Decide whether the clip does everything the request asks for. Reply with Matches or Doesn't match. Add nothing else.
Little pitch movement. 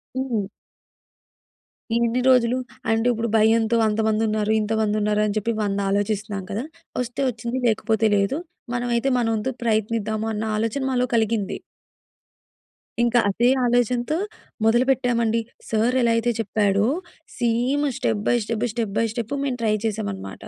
Matches